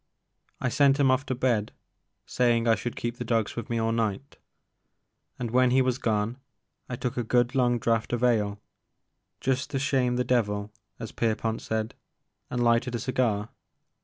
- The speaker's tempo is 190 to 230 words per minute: No, average, 180 wpm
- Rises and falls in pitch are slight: Yes, narrow, 2.0 semitones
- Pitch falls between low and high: No, low, 120 Hz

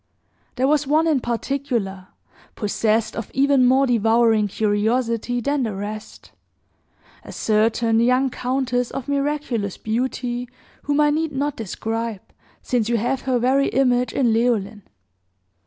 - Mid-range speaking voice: No, high, 245 Hz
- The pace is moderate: No, slow, 130 wpm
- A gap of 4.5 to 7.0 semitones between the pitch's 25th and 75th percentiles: No, average, 3.3 semitones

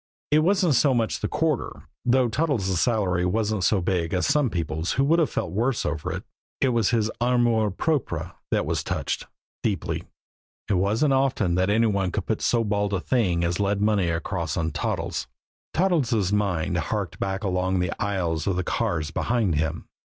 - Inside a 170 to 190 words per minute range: Yes, average, 180 wpm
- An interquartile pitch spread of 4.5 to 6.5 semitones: Yes, average, 5.1 semitones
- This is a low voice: Yes, low, 100 Hz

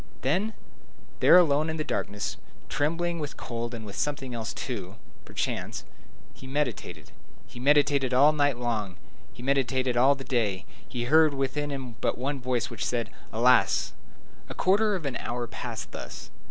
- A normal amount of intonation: Yes, average, 3.6 semitones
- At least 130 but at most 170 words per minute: Yes, average, 165 wpm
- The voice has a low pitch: Yes, low, 130 Hz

